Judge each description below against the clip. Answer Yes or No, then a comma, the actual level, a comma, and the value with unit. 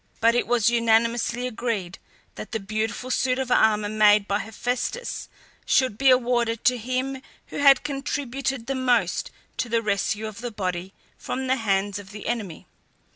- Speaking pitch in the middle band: No, high, 235 Hz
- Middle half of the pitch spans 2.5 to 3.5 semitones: Yes, average, 3.1 semitones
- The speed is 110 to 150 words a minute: No, average, 165 wpm